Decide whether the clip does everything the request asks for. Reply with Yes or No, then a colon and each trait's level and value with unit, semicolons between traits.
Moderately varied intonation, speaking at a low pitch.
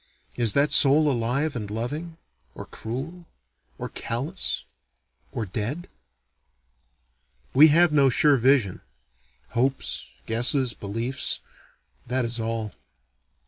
Yes: average, 4.4 semitones; low, 130 Hz